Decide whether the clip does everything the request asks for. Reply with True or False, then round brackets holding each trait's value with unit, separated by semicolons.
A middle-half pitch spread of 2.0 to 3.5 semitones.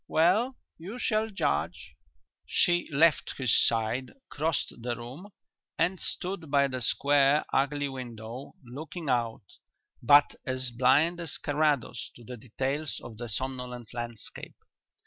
False (4.6 semitones)